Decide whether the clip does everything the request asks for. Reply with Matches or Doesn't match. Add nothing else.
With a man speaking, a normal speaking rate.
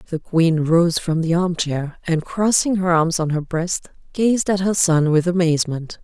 Doesn't match